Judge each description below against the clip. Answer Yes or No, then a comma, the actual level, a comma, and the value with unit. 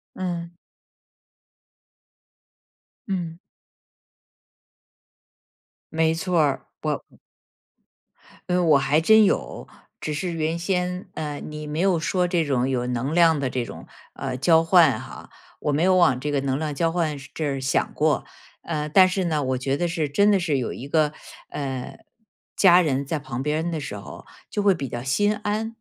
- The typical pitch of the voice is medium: Yes, medium, 160 Hz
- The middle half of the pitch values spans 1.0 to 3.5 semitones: No, average, 4.1 semitones